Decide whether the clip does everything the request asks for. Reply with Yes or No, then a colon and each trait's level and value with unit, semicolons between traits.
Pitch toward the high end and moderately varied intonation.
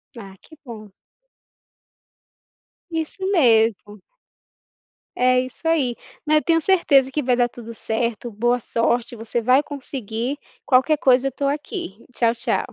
Yes: very high, 250 Hz; average, 3.7 semitones